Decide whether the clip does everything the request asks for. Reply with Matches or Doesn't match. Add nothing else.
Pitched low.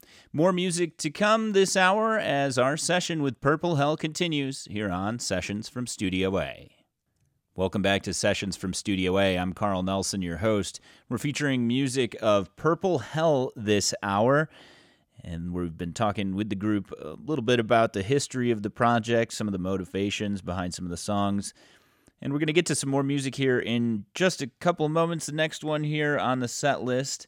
Matches